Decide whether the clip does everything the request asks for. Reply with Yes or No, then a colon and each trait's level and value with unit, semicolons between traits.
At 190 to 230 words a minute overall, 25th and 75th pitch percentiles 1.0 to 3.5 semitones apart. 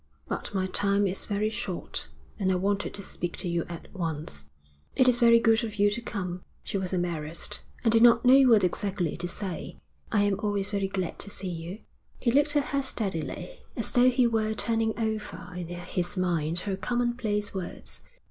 No: average, 195 wpm; average, 3.9 semitones